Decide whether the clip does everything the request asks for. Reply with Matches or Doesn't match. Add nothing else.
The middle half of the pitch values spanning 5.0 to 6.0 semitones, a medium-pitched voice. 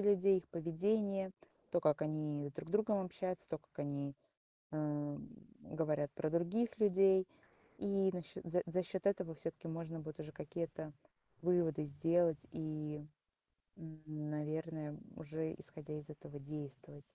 Doesn't match